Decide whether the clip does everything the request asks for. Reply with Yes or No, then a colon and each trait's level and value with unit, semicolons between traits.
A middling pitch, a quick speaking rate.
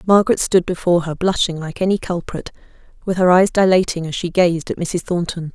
No: medium, 175 Hz; average, 195 wpm